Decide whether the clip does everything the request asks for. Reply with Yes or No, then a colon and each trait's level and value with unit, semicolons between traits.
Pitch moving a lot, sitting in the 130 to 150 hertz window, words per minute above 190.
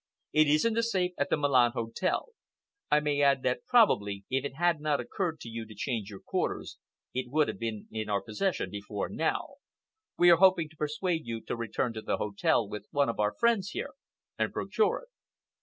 Yes: wide, 7.5 semitones; medium, 140 Hz; fast, 205 wpm